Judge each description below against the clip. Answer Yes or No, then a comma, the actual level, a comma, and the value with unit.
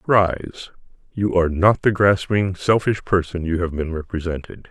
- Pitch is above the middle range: No, very low, 90 Hz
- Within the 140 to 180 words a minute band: Yes, average, 155 wpm